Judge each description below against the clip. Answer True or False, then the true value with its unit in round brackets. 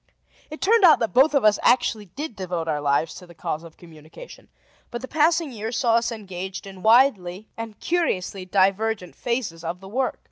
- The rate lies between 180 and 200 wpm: True (190 wpm)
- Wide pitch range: True (5.9 semitones)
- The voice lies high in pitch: True (210 Hz)